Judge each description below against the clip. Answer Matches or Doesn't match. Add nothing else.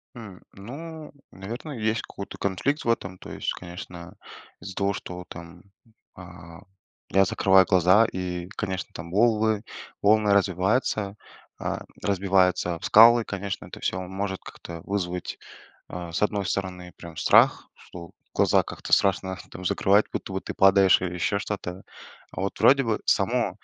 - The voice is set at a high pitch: Doesn't match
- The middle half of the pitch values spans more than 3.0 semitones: Doesn't match